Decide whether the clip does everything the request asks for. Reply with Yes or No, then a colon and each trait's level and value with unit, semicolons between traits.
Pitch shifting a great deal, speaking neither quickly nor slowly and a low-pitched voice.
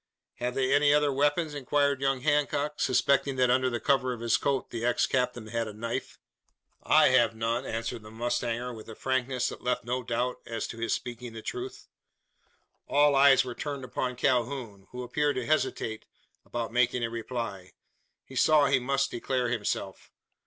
No: average, 2.7 semitones; average, 180 wpm; low, 125 Hz